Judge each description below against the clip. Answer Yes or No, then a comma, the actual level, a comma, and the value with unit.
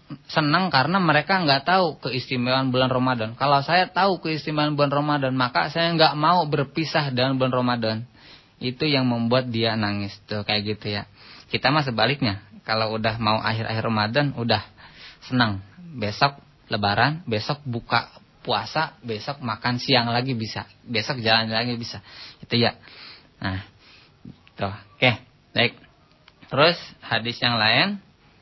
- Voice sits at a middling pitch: No, low, 125 Hz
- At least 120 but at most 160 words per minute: Yes, average, 135 wpm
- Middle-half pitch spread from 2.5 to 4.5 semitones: No, average, 5.0 semitones